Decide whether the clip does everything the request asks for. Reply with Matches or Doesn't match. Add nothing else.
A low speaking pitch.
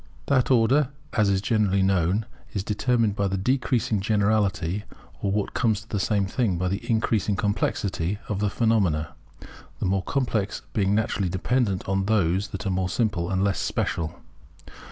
Matches